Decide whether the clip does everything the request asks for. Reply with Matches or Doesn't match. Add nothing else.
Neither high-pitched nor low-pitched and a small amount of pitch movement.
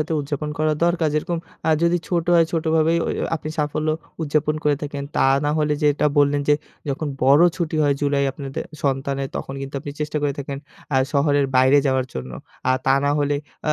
Matches